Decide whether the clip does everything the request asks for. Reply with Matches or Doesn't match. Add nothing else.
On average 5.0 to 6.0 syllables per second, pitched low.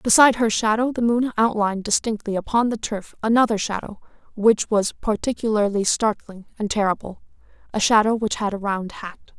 Doesn't match